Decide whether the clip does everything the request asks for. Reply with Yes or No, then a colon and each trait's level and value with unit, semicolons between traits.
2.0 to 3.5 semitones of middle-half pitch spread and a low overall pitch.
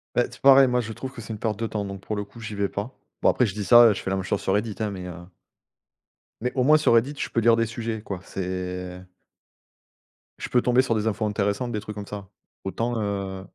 Yes: average, 2.9 semitones; low, 105 Hz